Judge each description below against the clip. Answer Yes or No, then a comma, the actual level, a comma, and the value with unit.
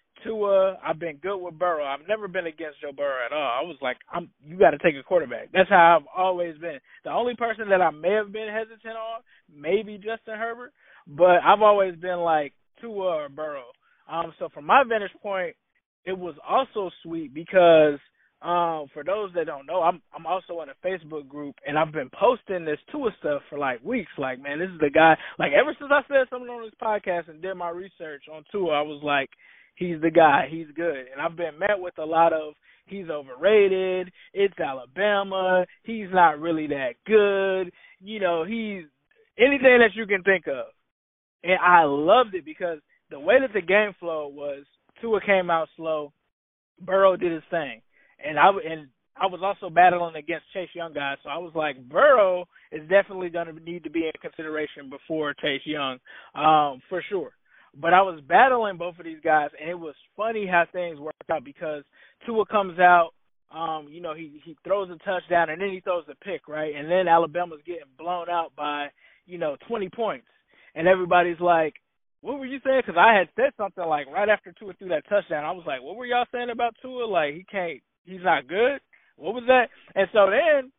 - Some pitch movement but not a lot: Yes, average, 4.6 semitones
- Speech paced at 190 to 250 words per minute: Yes, fast, 205 wpm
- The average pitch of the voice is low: No, medium, 180 Hz